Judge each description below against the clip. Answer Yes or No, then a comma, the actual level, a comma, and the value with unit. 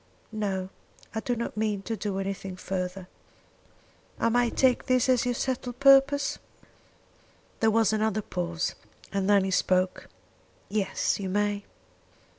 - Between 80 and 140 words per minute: Yes, slow, 135 wpm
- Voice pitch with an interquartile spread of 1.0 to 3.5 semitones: No, average, 4.0 semitones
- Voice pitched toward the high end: Yes, high, 210 Hz